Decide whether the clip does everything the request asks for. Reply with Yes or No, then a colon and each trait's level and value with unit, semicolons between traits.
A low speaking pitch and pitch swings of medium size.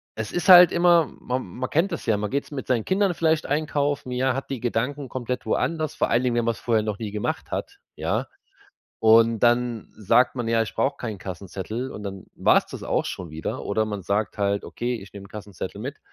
Yes: low, 120 Hz; average, 4.7 semitones